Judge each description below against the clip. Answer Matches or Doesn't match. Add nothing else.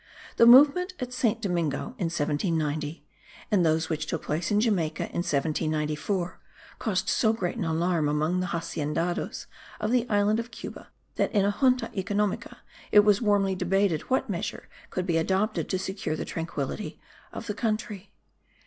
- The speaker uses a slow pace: Doesn't match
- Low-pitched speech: Doesn't match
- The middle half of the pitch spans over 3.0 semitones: Matches